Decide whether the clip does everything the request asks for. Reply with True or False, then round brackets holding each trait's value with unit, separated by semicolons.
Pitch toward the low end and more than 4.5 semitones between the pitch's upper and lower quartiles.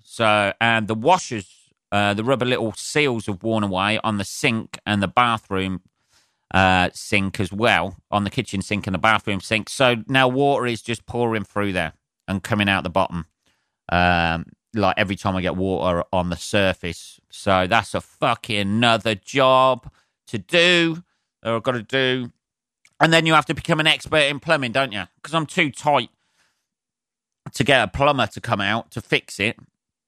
True (110 Hz; 5.1 semitones)